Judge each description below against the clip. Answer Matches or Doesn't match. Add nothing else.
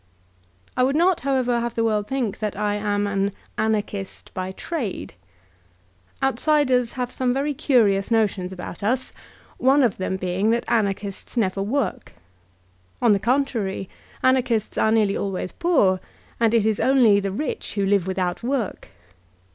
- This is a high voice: Matches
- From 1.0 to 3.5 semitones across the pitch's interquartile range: Doesn't match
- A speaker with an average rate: Matches